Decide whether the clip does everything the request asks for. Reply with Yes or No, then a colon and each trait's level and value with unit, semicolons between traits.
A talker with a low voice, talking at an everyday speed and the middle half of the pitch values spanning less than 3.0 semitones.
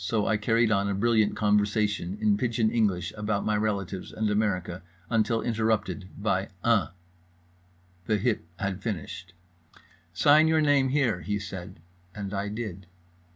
Yes: low, 105 Hz; average, 145 wpm; narrow, 2.4 semitones